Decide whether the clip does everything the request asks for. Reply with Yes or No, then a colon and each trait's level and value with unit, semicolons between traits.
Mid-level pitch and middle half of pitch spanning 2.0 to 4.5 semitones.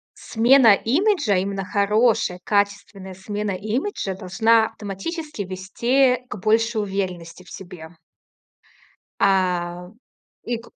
No: high, 205 Hz; average, 3.6 semitones